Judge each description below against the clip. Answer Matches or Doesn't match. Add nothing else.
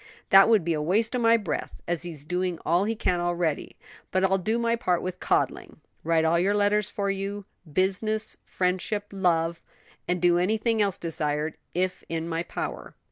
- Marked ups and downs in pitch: Doesn't match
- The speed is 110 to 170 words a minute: Doesn't match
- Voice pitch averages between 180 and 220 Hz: Matches